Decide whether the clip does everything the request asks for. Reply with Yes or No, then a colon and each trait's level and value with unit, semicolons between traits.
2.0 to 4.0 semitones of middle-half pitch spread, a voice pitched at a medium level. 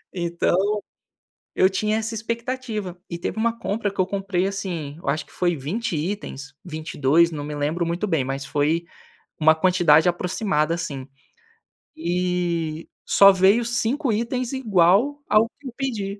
No: average, 5.0 semitones; medium, 180 Hz